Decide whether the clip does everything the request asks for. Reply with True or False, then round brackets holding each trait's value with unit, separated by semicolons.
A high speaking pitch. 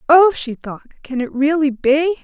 True (295 Hz)